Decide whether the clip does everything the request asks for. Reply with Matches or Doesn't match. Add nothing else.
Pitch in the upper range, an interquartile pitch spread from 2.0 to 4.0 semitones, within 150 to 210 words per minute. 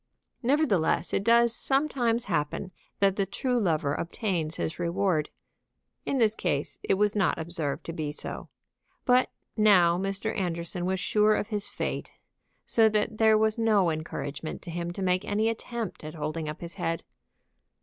Doesn't match